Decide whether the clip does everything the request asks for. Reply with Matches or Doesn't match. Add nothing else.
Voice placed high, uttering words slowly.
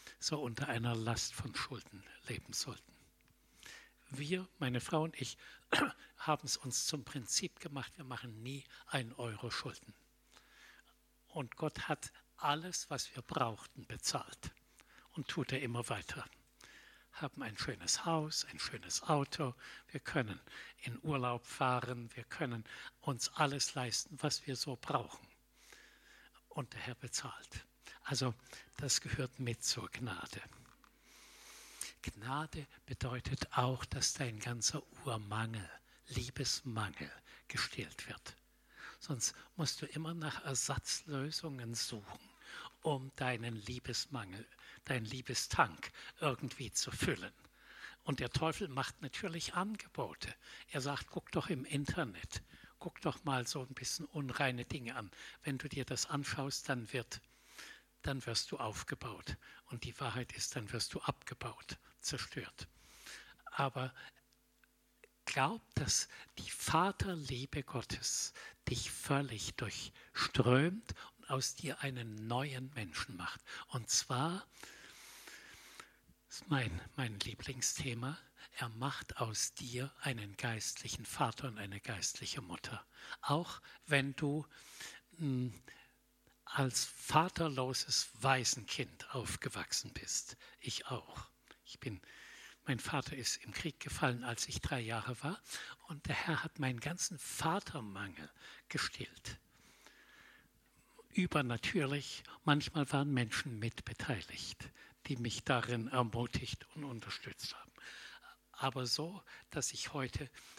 Doesn't match